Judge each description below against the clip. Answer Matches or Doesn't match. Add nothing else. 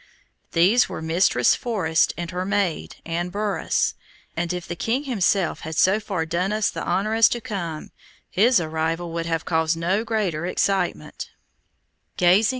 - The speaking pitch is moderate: Matches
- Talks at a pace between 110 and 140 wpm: Doesn't match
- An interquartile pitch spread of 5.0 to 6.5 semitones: Doesn't match